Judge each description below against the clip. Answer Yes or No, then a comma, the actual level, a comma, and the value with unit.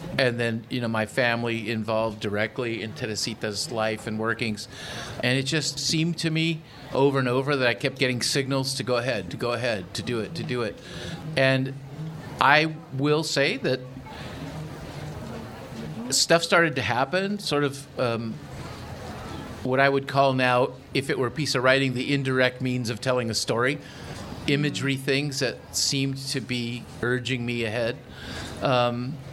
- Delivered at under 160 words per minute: No, average, 165 wpm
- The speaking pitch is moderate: No, low, 130 Hz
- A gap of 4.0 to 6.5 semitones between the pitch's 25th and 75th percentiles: No, average, 2.9 semitones